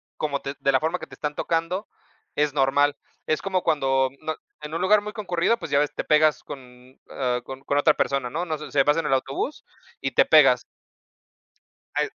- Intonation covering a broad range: No, average, 3.4 semitones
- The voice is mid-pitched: Yes, medium, 150 Hz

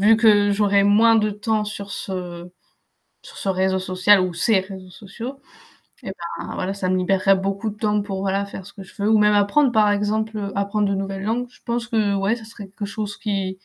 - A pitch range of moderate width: No, narrow, 1.8 semitones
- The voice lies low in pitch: No, high, 200 Hz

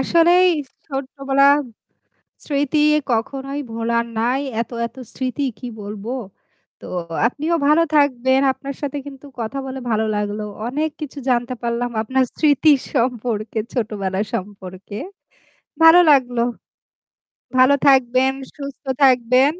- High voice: Yes, very high, 260 Hz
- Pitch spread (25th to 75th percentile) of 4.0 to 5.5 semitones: No, average, 3.2 semitones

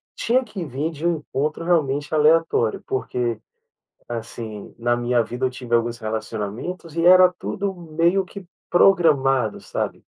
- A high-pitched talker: No, medium, 145 Hz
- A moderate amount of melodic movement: No, wide, 6.2 semitones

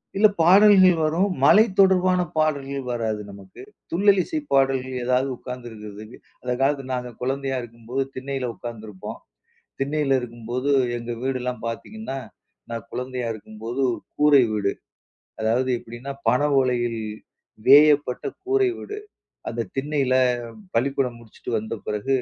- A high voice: No, low, 130 Hz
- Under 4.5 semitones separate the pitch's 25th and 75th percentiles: Yes, average, 3.9 semitones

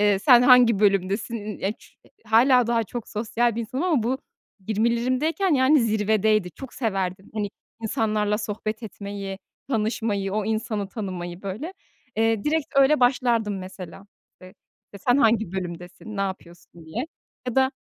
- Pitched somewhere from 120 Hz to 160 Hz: No, high, 220 Hz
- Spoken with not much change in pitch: No, average, 3.5 semitones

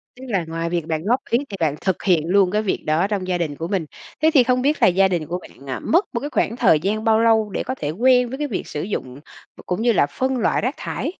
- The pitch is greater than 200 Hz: No, high, 195 Hz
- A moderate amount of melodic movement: No, wide, 6.4 semitones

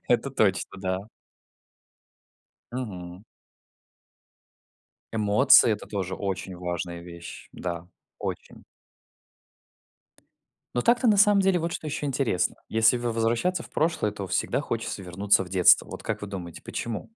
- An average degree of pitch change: No, wide, 6.5 semitones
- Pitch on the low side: Yes, low, 105 Hz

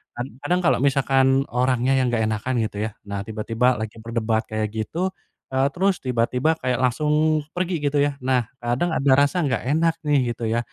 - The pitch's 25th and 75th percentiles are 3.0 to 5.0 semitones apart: Yes, average, 3.6 semitones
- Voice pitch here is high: No, low, 125 Hz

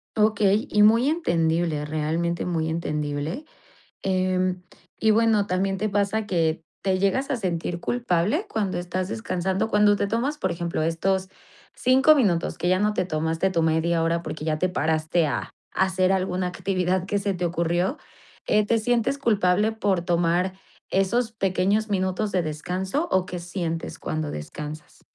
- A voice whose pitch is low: No, medium, 185 Hz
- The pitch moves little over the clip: No, average, 3.6 semitones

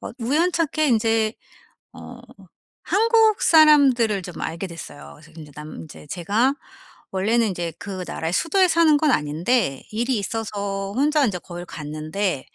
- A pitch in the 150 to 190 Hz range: No, high, 215 Hz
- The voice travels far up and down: Yes, wide, 8.8 semitones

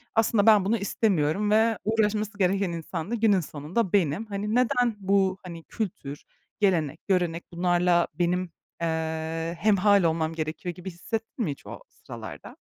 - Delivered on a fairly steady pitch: No, average, 4.1 semitones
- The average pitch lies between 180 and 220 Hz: Yes, medium, 185 Hz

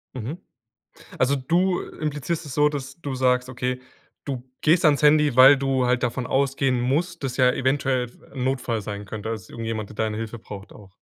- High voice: No, low, 130 Hz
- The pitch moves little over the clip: No, average, 3.1 semitones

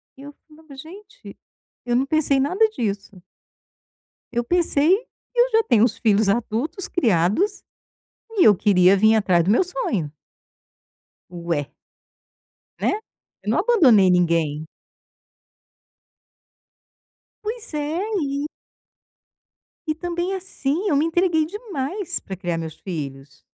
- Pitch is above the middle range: Yes, very high, 275 Hz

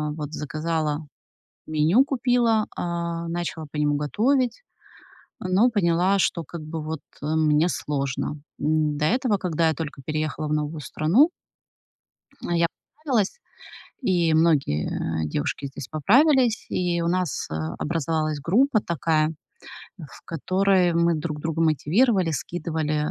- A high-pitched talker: No, medium, 165 Hz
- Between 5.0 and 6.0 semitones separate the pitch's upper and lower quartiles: No, average, 3.5 semitones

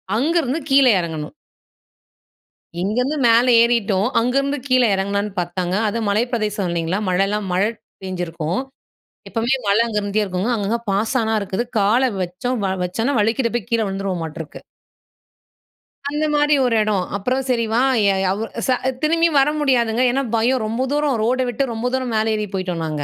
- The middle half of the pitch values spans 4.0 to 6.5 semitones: Yes, average, 4.6 semitones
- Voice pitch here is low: No, high, 220 Hz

